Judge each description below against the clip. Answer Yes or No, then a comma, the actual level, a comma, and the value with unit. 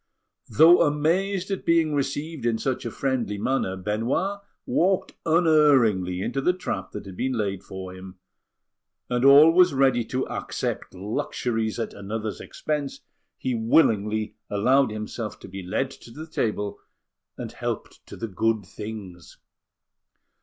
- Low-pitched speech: Yes, low, 120 Hz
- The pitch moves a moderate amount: No, wide, 6.2 semitones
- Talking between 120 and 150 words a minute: Yes, average, 140 wpm